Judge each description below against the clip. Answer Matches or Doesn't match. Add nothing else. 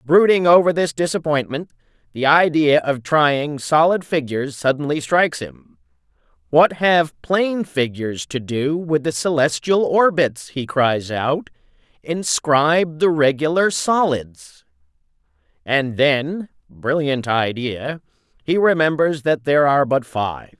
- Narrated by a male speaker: Matches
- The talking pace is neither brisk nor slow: Doesn't match